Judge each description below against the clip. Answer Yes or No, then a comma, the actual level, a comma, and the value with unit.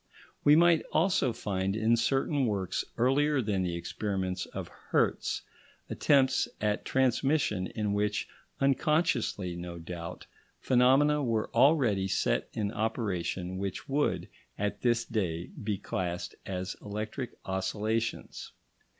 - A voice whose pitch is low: Yes, low, 110 Hz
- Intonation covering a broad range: Yes, wide, 5.8 semitones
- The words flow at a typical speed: No, slow, 115 wpm